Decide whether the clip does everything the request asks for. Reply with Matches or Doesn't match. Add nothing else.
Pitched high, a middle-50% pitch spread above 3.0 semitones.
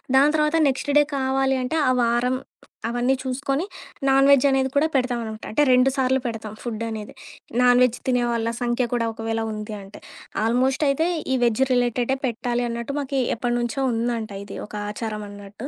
Doesn't match